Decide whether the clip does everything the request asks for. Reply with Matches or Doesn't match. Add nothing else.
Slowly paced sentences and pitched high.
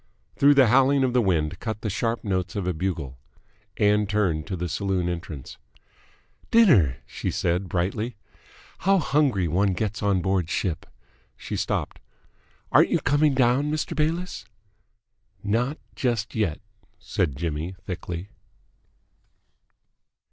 Doesn't match